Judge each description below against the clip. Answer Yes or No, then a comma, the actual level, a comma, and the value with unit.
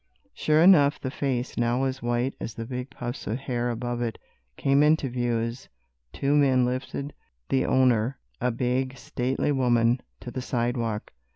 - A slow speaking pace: No, average, 165 wpm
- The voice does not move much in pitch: Yes, narrow, 2.0 semitones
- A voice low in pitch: Yes, low, 125 Hz